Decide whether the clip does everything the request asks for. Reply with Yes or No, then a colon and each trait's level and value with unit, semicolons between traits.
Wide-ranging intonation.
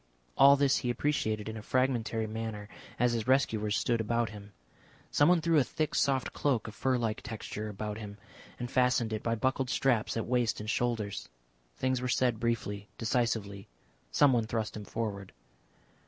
No: average, 3.0 semitones